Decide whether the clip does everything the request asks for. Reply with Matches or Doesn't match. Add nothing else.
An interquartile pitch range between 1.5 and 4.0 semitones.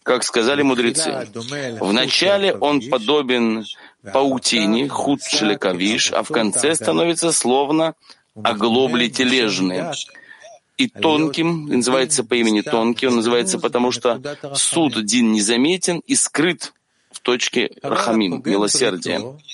Doesn't match